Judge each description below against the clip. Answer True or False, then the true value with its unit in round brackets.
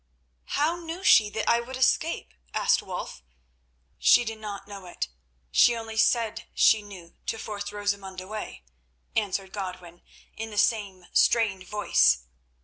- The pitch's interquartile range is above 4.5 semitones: False (2.9 semitones)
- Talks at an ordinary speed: True (145 wpm)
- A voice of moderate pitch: False (210 Hz)